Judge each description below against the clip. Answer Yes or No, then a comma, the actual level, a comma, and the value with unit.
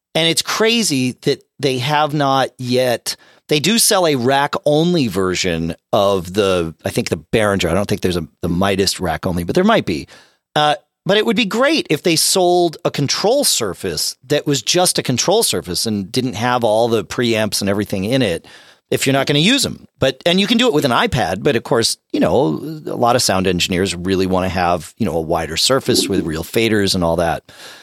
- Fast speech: Yes, fast, 220 wpm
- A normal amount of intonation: No, wide, 8.1 semitones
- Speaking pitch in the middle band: No, low, 125 Hz